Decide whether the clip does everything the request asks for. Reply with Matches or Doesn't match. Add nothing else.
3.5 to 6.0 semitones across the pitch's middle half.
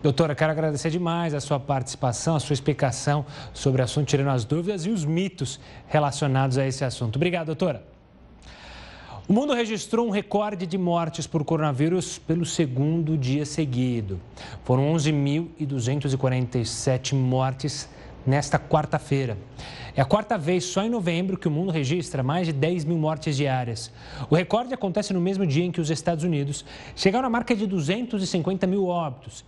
Matches